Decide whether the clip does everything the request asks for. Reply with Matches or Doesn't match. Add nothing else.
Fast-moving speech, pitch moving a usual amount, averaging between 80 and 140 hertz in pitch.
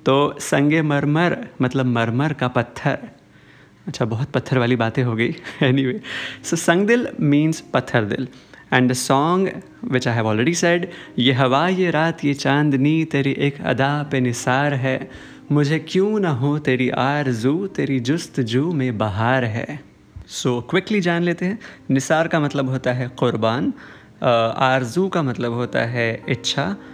Doesn't match